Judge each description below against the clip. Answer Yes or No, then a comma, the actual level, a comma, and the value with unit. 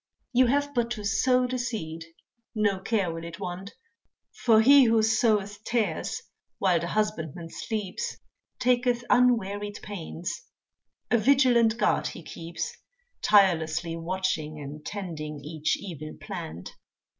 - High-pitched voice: Yes, high, 205 Hz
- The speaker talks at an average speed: No, slow, 125 wpm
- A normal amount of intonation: No, wide, 5.8 semitones